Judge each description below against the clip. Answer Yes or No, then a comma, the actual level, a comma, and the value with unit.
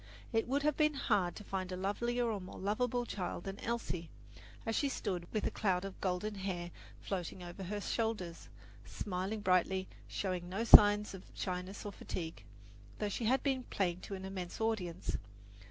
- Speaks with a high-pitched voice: Yes, high, 195 Hz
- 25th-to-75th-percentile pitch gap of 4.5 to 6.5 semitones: No, average, 3.5 semitones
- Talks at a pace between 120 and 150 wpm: No, average, 175 wpm